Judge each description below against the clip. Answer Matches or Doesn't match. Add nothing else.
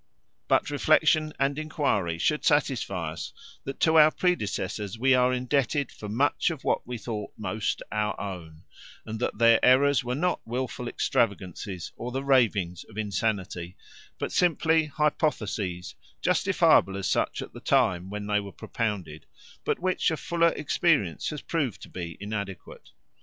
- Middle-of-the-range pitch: Doesn't match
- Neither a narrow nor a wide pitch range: Doesn't match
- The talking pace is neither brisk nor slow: Matches